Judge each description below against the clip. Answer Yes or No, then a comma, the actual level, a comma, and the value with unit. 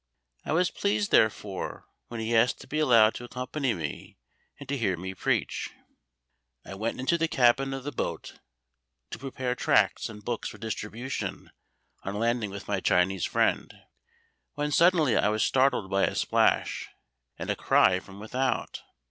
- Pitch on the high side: No, low, 115 Hz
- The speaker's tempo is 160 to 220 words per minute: Yes, average, 165 wpm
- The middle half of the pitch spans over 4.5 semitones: Yes, average, 4.9 semitones